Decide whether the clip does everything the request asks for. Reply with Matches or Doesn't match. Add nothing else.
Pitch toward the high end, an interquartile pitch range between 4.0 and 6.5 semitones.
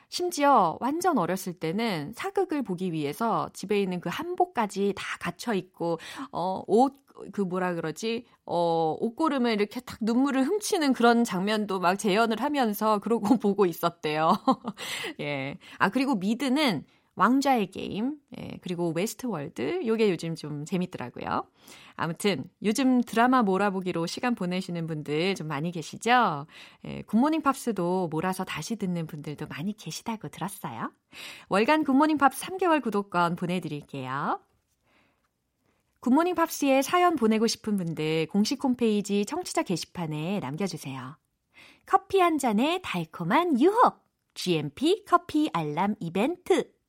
Doesn't match